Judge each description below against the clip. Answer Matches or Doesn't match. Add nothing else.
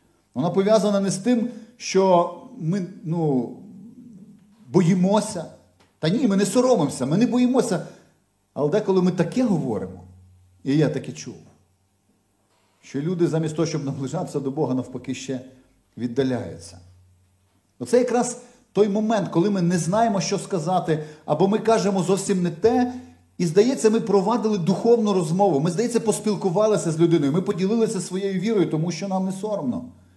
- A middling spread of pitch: Doesn't match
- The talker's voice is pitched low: Doesn't match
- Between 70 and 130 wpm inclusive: Doesn't match